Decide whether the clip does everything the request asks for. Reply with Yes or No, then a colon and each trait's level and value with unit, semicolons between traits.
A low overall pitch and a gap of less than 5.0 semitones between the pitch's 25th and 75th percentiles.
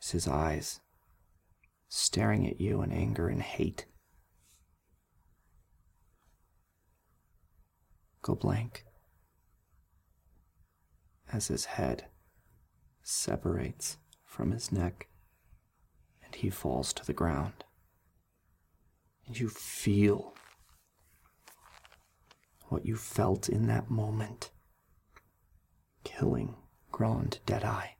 Yes: very low, 90 Hz; average, 4.1 semitones